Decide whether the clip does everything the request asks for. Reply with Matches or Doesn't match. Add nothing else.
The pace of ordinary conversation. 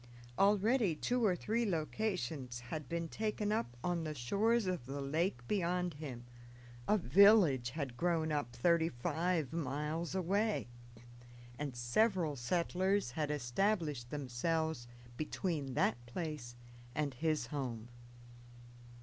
Doesn't match